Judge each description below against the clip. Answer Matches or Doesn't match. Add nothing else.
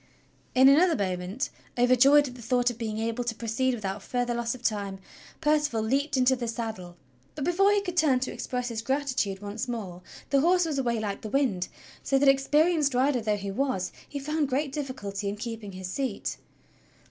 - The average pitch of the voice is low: Doesn't match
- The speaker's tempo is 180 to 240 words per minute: Matches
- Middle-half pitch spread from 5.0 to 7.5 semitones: Doesn't match